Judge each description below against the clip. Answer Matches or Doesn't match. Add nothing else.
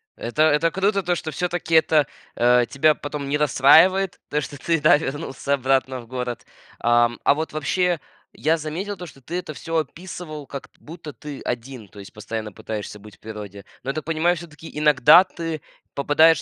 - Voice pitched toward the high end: Doesn't match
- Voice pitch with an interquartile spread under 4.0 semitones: Doesn't match